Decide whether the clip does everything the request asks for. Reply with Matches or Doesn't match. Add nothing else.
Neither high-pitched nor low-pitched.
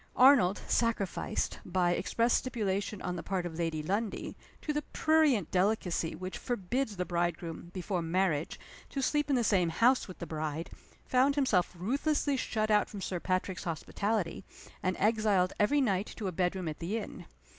Doesn't match